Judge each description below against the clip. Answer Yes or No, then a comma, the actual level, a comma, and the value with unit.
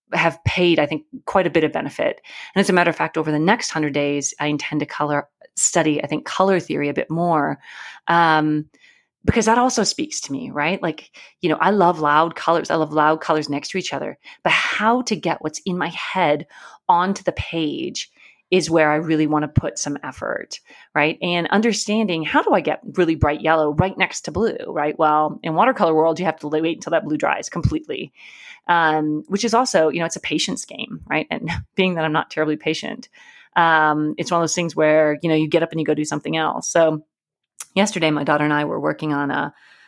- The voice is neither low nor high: Yes, medium, 160 Hz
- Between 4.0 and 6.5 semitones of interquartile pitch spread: No, average, 3.0 semitones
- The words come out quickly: Yes, fast, 225 wpm